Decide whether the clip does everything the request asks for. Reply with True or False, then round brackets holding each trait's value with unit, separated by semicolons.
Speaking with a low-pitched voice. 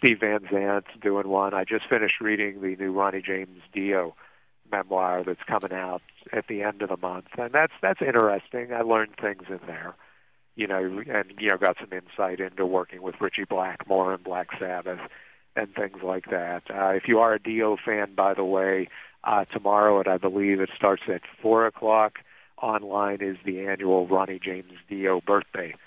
True (95 Hz)